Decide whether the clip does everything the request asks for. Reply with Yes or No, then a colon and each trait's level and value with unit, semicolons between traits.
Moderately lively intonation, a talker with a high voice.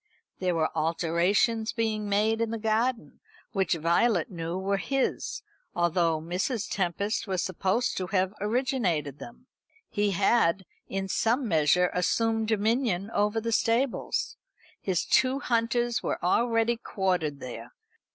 Yes: average, 4.5 semitones; high, 200 Hz